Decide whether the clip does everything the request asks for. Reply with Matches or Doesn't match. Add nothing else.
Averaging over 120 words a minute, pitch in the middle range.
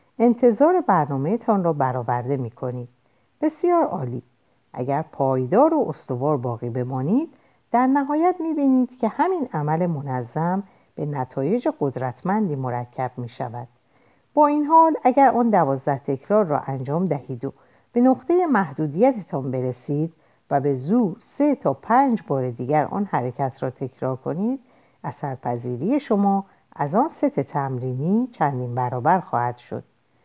Matches